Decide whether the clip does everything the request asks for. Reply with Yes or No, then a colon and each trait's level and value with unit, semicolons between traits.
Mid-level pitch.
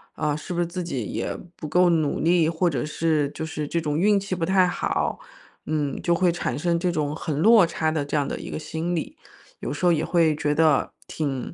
Yes: medium, 160 Hz